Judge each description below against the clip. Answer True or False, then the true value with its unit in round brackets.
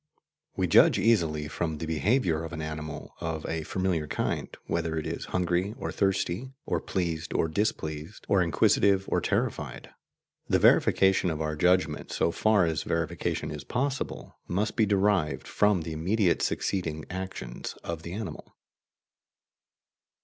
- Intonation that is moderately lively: True (3.7 semitones)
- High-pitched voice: False (85 Hz)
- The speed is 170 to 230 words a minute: False (145 wpm)